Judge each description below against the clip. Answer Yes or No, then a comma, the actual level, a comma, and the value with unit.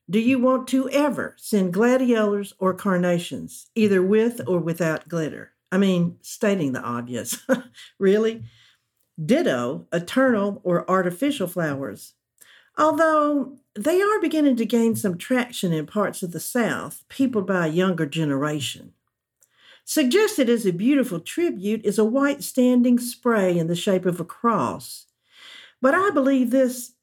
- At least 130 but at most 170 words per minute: Yes, average, 140 wpm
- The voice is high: Yes, high, 215 Hz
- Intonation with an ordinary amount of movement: No, wide, 6.7 semitones